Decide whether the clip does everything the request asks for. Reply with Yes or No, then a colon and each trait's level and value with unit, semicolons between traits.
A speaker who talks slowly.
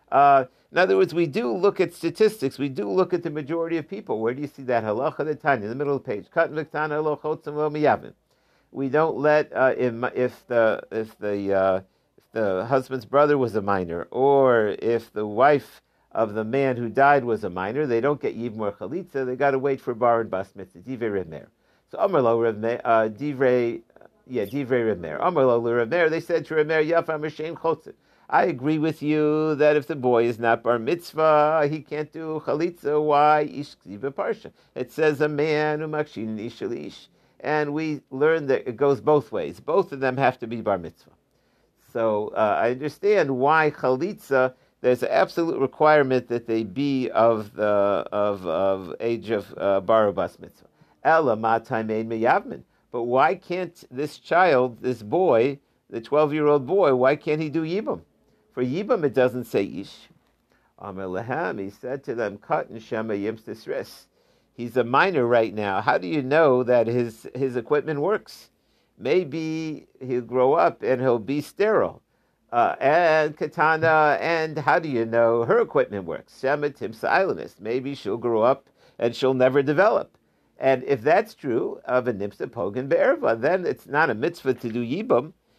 No: average, 165 wpm